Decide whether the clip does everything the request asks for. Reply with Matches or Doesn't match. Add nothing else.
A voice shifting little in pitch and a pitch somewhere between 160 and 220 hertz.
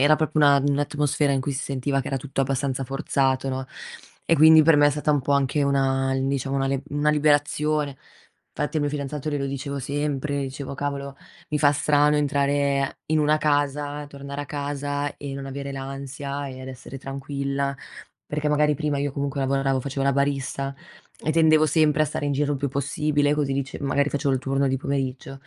Doesn't match